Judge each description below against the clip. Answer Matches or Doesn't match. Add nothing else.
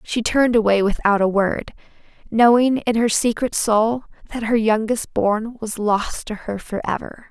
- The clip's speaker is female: Matches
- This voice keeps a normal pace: Matches